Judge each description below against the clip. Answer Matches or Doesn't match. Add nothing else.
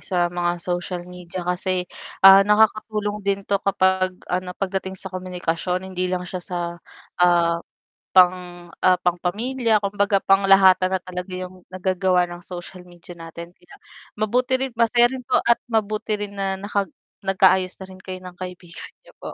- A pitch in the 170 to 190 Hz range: Matches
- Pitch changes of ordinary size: Doesn't match